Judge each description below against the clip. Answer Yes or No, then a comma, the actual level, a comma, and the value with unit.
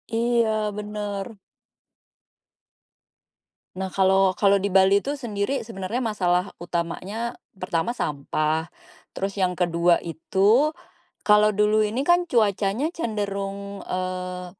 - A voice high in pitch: Yes, high, 200 Hz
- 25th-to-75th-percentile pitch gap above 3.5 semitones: No, average, 2.9 semitones